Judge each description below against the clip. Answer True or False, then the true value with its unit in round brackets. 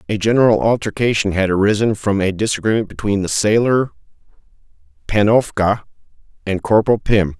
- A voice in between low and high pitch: False (105 Hz)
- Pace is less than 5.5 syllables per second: False (5.7 syllables/s)